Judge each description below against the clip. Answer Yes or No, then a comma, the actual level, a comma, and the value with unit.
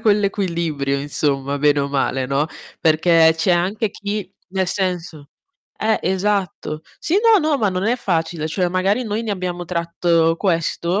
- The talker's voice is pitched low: No, medium, 175 Hz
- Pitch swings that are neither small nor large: Yes, average, 4.1 semitones